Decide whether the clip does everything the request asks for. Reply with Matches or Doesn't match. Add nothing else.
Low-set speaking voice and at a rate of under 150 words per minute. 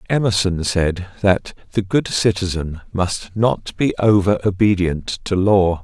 Matches